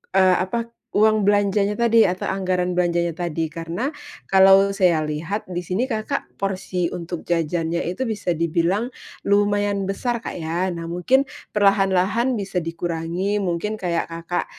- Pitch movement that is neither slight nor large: Yes, average, 3.2 semitones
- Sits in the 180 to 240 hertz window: Yes, medium, 185 Hz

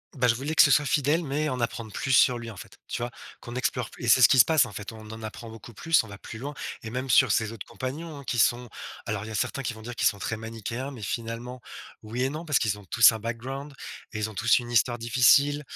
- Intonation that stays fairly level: No, average, 3.1 semitones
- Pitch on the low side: Yes, low, 120 Hz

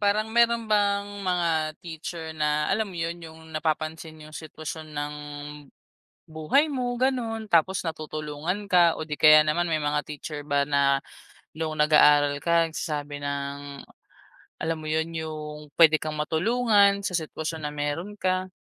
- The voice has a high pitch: No, medium, 160 Hz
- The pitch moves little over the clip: No, average, 3.4 semitones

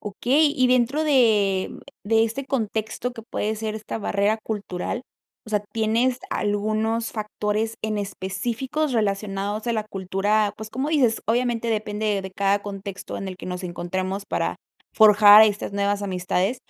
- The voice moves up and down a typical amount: No, narrow, 2.3 semitones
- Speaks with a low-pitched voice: No, high, 215 Hz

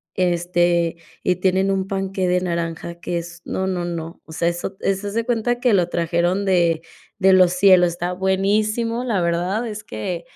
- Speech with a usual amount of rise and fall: No, narrow, 2.3 semitones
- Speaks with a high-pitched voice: No, medium, 180 Hz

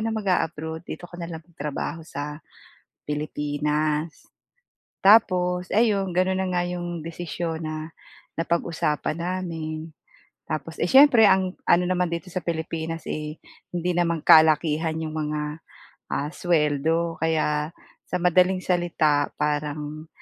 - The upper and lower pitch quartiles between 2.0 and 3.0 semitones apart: Yes, narrow, 2.6 semitones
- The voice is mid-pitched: Yes, medium, 165 Hz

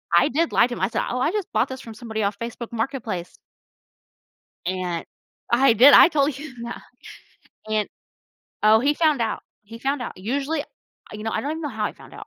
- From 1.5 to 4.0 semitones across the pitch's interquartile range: No, average, 4.5 semitones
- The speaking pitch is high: Yes, high, 235 Hz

